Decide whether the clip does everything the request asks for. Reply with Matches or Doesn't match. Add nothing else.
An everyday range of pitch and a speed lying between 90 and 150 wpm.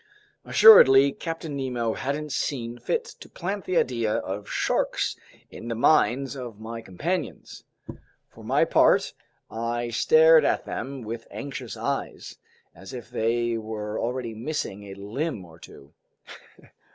Matches